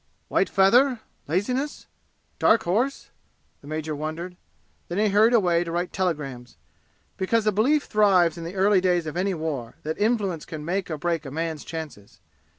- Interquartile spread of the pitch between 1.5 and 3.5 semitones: No, average, 4.7 semitones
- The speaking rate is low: No, average, 165 wpm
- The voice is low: No, medium, 180 Hz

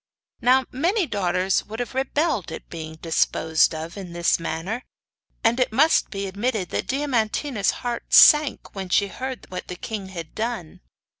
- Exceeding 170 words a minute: No, average, 160 wpm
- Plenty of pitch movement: Yes, wide, 6.2 semitones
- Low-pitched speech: No, high, 210 Hz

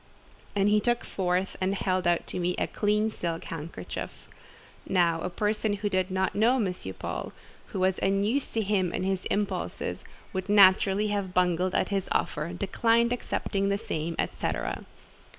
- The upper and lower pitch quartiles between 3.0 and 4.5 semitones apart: No, narrow, 2.4 semitones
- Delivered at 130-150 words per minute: No, average, 160 wpm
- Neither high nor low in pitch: No, high, 195 Hz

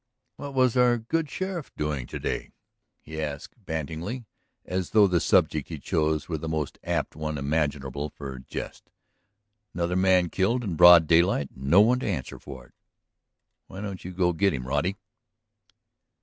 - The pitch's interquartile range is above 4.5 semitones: Yes, average, 5.0 semitones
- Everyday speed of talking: Yes, average, 165 wpm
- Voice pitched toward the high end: No, very low, 85 Hz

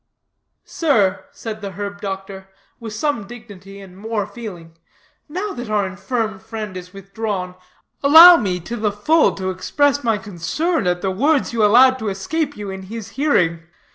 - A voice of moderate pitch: No, high, 210 Hz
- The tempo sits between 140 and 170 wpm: Yes, average, 165 wpm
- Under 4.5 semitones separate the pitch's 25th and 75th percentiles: Yes, average, 4.1 semitones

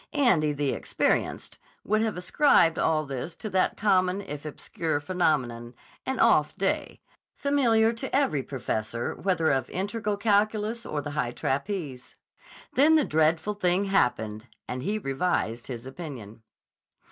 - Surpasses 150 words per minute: No, slow, 135 wpm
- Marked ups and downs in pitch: Yes, wide, 7.6 semitones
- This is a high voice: No, medium, 170 Hz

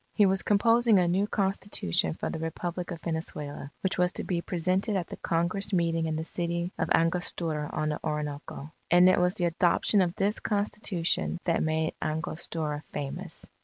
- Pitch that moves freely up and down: No, average, 3.0 semitones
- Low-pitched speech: No, medium, 170 Hz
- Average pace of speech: Yes, average, 175 wpm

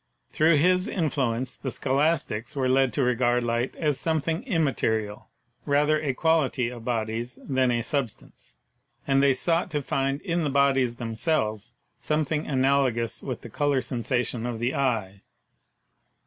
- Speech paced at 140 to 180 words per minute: Yes, average, 155 wpm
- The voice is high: No, low, 135 Hz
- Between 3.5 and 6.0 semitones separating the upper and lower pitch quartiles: Yes, average, 3.8 semitones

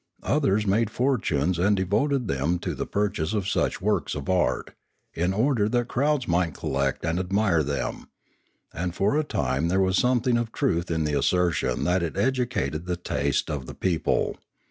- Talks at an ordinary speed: Yes, average, 175 wpm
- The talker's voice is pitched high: No, very low, 95 Hz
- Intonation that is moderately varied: No, wide, 5.9 semitones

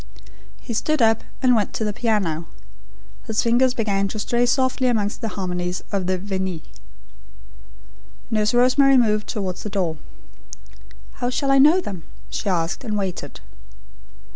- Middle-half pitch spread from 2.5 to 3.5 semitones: No, average, 4.3 semitones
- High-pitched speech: Yes, high, 215 Hz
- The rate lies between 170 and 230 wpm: No, average, 145 wpm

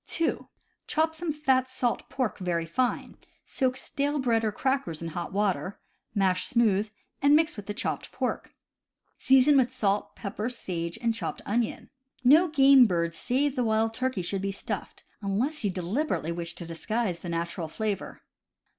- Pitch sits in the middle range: No, high, 225 Hz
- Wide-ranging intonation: Yes, wide, 6.1 semitones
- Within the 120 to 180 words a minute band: Yes, average, 165 wpm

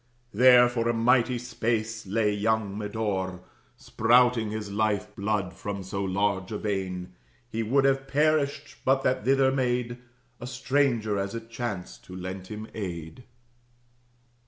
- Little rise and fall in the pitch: No, average, 3.7 semitones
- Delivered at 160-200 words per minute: No, average, 140 wpm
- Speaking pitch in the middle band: No, low, 110 Hz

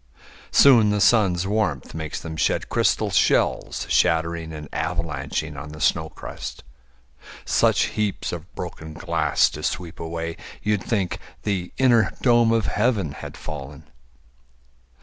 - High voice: No, very low, 85 Hz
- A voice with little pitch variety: No, average, 4.8 semitones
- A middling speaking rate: No, slow, 130 wpm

